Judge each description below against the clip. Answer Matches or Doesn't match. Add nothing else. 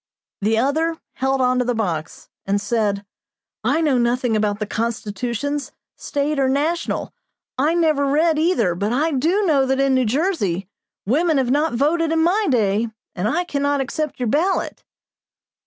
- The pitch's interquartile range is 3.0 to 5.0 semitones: Doesn't match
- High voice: Matches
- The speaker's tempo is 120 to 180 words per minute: Matches